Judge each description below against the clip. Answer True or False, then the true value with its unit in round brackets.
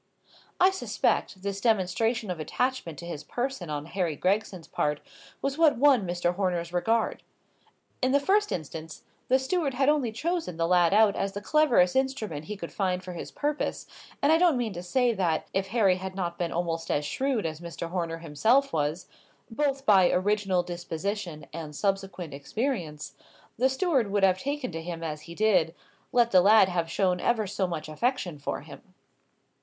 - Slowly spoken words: False (180 wpm)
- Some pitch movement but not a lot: False (6.4 semitones)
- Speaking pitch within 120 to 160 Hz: False (190 Hz)